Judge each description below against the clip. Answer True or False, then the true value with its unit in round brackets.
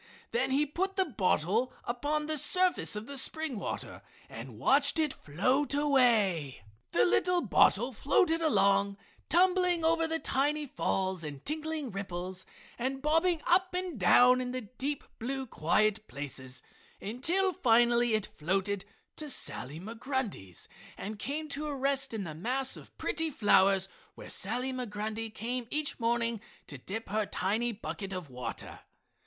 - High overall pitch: True (245 Hz)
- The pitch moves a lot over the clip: True (7.0 semitones)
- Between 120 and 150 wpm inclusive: True (145 wpm)